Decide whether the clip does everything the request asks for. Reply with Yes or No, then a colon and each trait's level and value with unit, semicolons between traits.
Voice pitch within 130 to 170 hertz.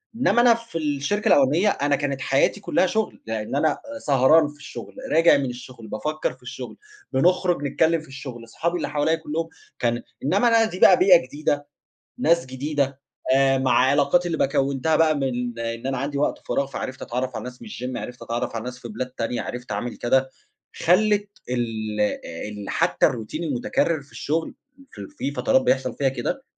Yes: medium, 140 Hz